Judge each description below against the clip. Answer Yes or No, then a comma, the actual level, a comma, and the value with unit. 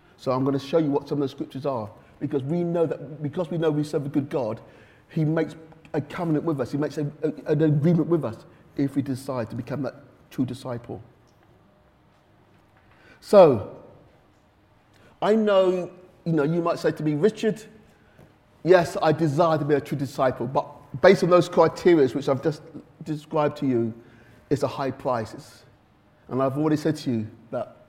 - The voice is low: No, medium, 150 Hz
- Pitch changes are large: No, average, 3.5 semitones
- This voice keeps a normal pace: Yes, average, 190 wpm